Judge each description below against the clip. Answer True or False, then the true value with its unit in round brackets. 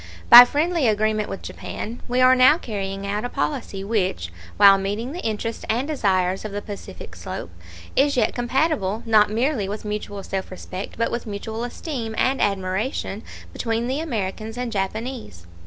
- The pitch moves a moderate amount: True (3.9 semitones)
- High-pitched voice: True (220 Hz)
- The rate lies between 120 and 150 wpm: False (165 wpm)